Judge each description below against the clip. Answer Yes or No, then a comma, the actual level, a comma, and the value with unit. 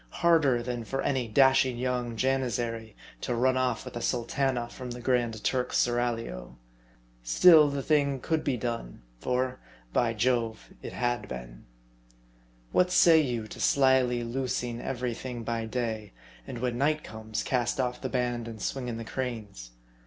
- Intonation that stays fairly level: Yes, narrow, 2.2 semitones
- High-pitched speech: No, low, 125 Hz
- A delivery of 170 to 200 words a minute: No, average, 160 wpm